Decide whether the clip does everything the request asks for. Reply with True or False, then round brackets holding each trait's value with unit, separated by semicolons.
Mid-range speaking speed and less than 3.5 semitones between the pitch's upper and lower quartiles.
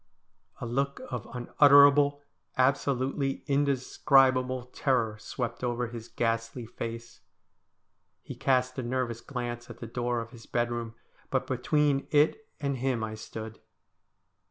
False (125 wpm; 2.6 semitones)